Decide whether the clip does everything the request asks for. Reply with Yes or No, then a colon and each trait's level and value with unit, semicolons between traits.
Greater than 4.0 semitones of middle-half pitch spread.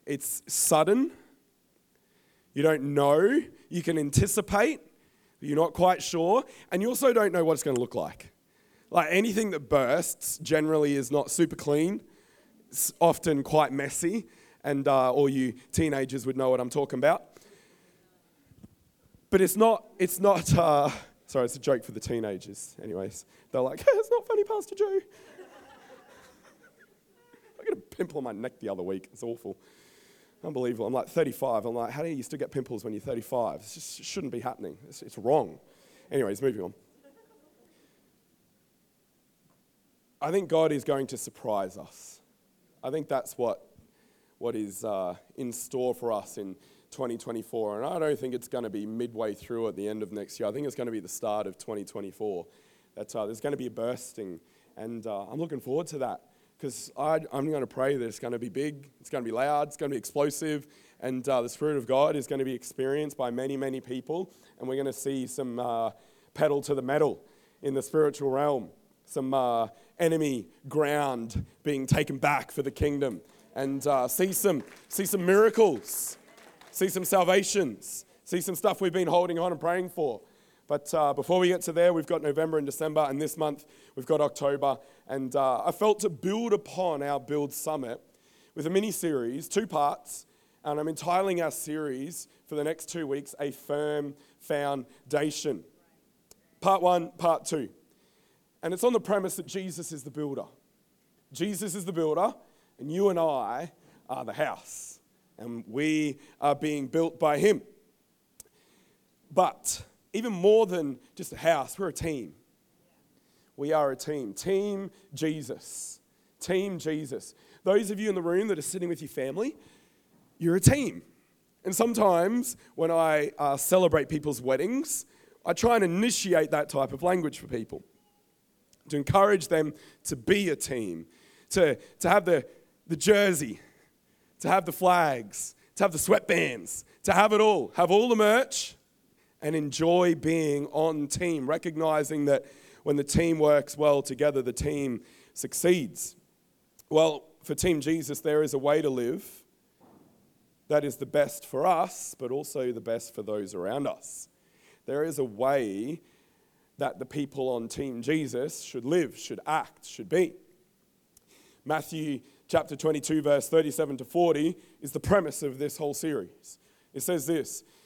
Yes: average, 4.4 semitones